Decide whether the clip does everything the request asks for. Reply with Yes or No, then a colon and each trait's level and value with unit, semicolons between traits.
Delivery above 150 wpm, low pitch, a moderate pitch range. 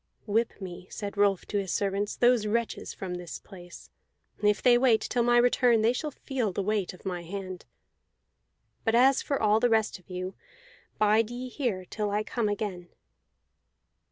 No: average, 175 wpm; high, 210 Hz; average, 3.8 semitones